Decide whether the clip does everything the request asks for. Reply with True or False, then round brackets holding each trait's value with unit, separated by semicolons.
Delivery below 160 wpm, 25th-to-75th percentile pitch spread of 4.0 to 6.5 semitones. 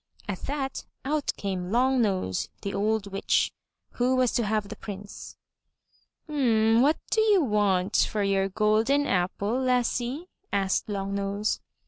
True (140 wpm; 4.4 semitones)